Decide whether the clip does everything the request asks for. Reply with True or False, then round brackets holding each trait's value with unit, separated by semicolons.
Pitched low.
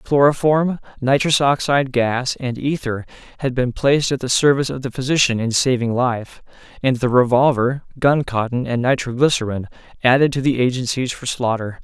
True (130 Hz)